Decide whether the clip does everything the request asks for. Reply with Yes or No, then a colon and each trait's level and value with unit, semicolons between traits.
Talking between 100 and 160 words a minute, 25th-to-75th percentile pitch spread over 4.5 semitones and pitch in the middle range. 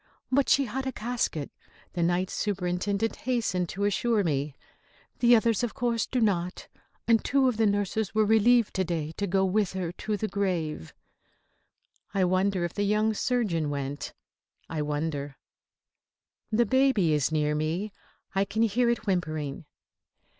No: average, 155 wpm; average, 5.0 semitones; high, 200 Hz